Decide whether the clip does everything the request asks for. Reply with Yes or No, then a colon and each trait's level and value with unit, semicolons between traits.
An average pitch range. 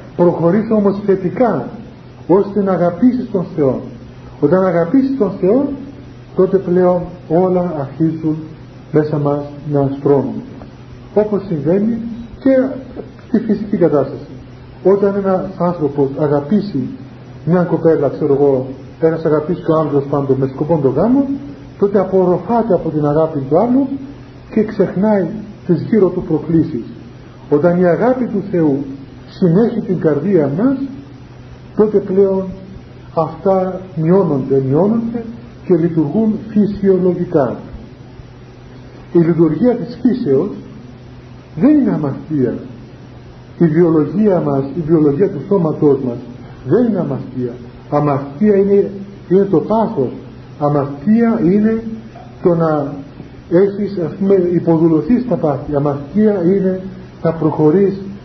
No: wide, 6.0 semitones